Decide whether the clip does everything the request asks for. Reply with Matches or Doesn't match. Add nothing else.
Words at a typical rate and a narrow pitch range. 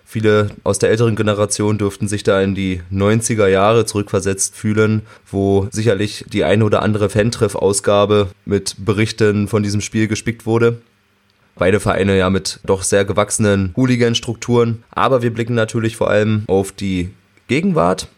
Matches